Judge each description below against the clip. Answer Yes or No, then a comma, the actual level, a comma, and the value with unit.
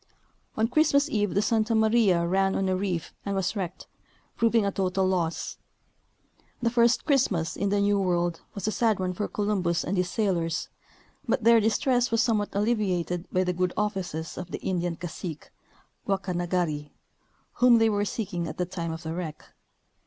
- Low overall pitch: No, high, 195 Hz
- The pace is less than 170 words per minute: No, average, 175 wpm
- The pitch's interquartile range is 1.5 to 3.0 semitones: No, average, 3.8 semitones